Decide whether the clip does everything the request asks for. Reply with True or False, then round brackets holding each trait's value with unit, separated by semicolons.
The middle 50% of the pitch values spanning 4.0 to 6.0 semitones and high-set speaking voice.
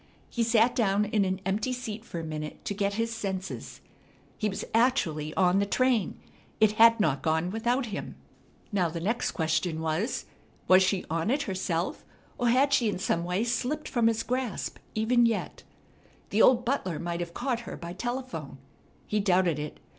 True (5.2 semitones; 205 Hz)